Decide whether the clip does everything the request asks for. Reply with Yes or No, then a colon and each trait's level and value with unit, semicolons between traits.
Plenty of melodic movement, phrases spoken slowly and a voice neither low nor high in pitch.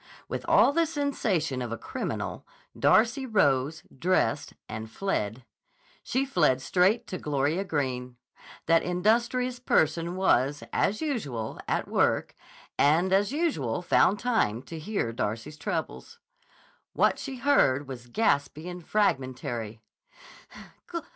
Yes: wide, 9.0 semitones; slow, 120 wpm; medium, 165 Hz